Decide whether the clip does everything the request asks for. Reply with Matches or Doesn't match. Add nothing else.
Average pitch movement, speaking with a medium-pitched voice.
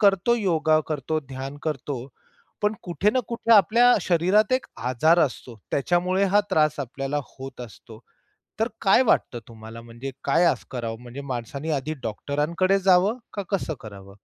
Doesn't match